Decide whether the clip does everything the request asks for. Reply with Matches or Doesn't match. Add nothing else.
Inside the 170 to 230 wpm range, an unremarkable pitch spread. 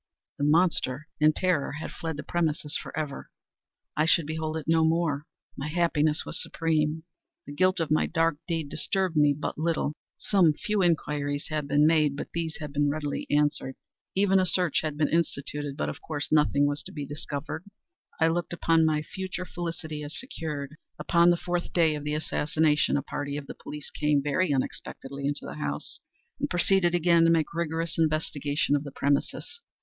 Doesn't match